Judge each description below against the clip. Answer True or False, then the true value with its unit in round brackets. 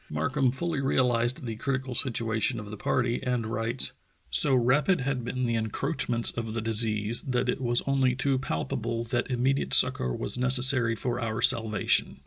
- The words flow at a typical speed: True (170 wpm)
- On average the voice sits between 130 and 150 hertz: False (120 Hz)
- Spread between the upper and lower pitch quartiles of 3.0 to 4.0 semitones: False (2.5 semitones)